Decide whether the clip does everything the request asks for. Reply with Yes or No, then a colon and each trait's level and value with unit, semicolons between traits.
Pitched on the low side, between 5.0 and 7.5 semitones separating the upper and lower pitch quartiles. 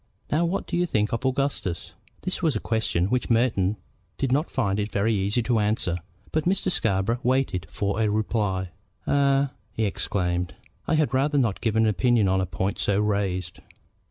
Yes: low, 110 Hz; wide, 5.4 semitones